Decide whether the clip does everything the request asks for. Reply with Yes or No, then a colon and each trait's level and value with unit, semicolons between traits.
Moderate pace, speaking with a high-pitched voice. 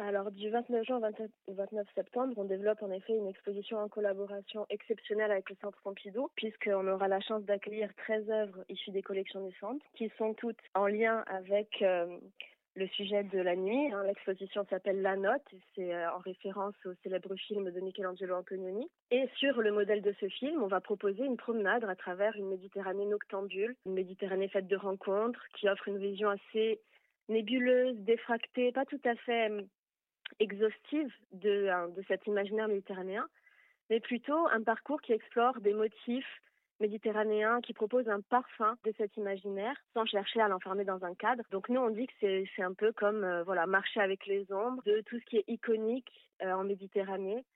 Yes: average, 185 wpm; high, 205 Hz